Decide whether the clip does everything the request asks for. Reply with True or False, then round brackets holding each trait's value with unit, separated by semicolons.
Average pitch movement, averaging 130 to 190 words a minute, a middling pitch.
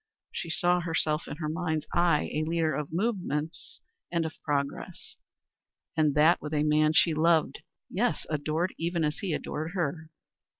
False (1.9 semitones; 160 wpm; 160 Hz)